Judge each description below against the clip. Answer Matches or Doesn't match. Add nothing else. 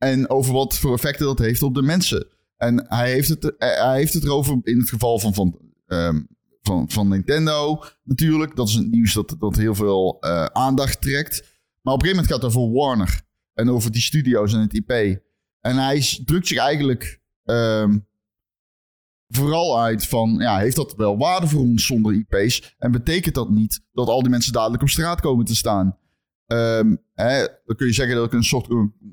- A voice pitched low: Matches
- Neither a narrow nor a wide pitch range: Matches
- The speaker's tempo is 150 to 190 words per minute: Doesn't match